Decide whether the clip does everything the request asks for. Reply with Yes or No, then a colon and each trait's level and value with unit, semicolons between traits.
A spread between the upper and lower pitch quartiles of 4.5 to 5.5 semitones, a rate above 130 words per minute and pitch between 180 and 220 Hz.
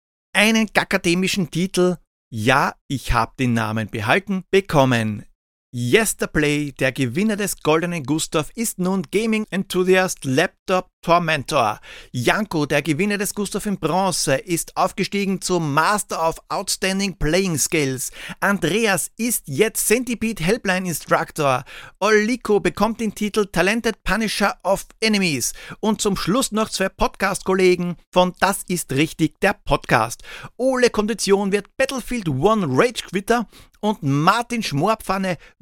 No: average, 4.9 semitones; slow, 125 wpm; medium, 185 Hz